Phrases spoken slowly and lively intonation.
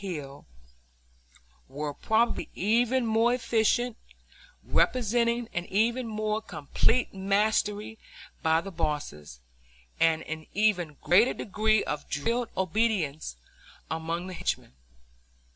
Yes: slow, 100 wpm; wide, 6.0 semitones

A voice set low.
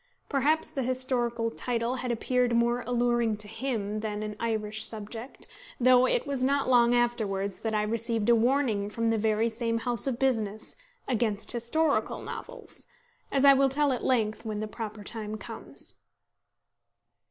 No: high, 235 Hz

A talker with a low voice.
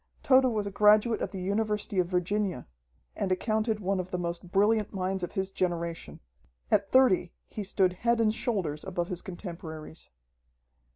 No: high, 190 Hz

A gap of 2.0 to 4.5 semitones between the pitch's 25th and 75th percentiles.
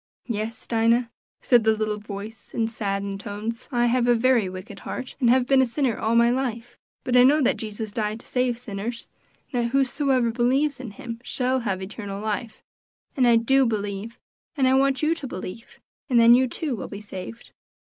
Yes: average, 3.1 semitones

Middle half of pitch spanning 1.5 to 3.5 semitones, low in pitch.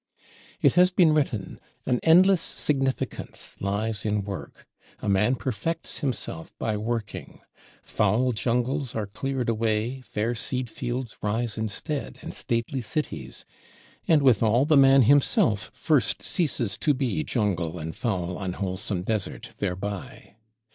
No: average, 4.6 semitones; low, 115 Hz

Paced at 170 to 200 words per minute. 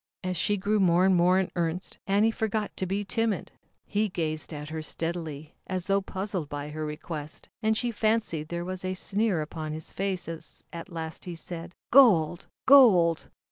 Yes: average, 180 wpm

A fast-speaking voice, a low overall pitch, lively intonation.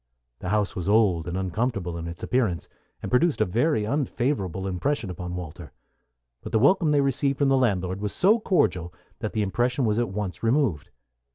No: average, 185 wpm; low, 105 Hz; wide, 6.5 semitones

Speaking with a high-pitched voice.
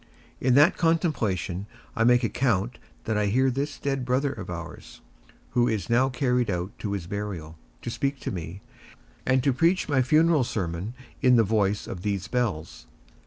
No: low, 120 Hz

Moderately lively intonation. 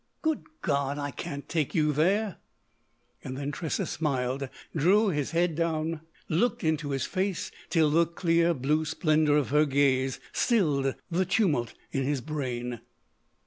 Yes: average, 3.3 semitones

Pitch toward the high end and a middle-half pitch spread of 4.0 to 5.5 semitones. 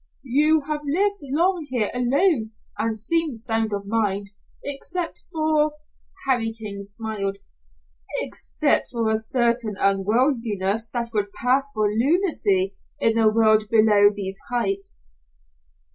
Yes: high, 225 Hz; average, 5.0 semitones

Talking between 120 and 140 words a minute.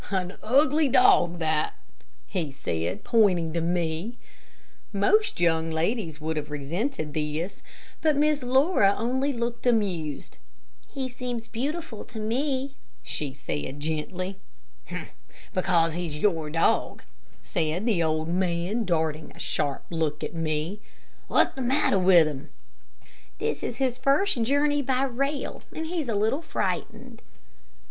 Yes: slow, 135 wpm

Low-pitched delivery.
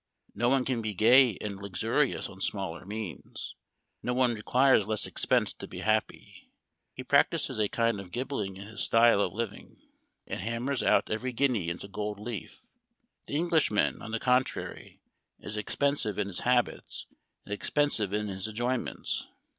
Yes: low, 110 Hz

